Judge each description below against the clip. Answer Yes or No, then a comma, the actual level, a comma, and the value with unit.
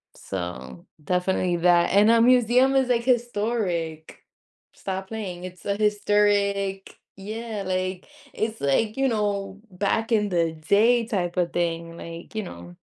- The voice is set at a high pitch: Yes, high, 200 Hz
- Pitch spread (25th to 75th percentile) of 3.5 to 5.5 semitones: Yes, average, 4.1 semitones